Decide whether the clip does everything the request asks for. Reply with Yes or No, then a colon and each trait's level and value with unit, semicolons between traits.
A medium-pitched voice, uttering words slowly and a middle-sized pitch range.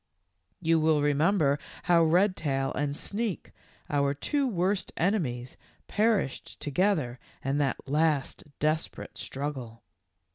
Yes: medium, 150 Hz; slow, 110 wpm; average, 4.7 semitones